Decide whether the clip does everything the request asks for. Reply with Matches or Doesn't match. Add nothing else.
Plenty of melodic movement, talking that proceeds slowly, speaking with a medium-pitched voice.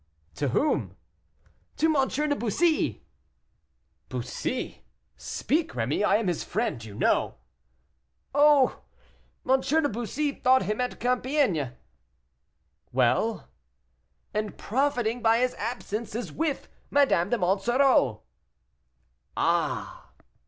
Doesn't match